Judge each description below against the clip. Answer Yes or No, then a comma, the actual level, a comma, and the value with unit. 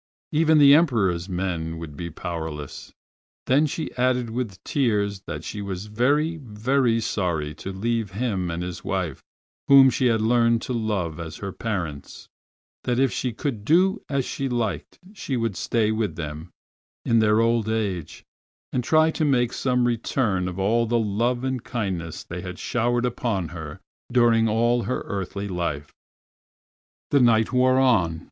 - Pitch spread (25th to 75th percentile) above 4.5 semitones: Yes, average, 5.3 semitones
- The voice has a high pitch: No, low, 110 Hz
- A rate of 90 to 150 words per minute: No, average, 160 wpm